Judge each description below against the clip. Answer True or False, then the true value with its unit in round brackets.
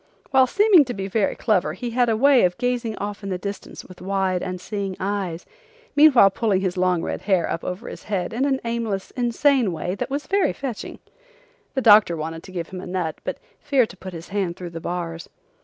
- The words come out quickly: True (215 wpm)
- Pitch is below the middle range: False (200 Hz)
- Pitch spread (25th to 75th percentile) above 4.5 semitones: True (4.9 semitones)